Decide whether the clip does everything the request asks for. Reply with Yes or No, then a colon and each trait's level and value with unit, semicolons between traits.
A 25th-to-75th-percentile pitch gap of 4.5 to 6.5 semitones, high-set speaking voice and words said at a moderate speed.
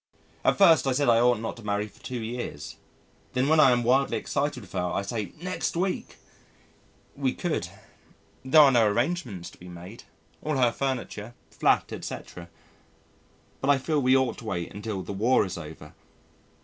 No: average, 5.1 semitones; low, 120 Hz; average, 180 wpm